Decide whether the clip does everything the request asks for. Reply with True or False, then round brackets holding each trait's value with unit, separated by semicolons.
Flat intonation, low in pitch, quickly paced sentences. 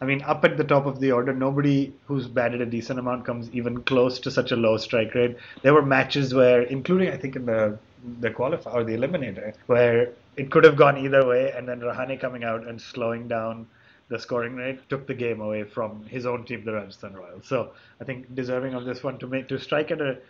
True (2.2 semitones; 125 Hz; 235 wpm)